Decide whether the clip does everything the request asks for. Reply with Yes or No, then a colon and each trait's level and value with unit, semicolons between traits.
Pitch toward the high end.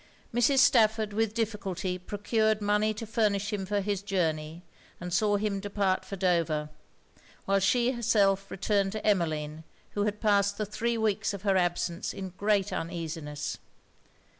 Yes: high, 200 Hz